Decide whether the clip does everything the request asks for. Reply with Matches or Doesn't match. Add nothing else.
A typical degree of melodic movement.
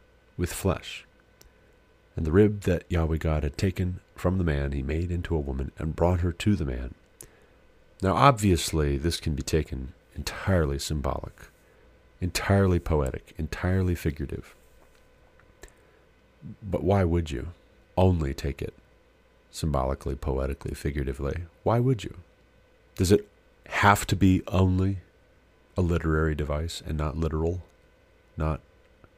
Matches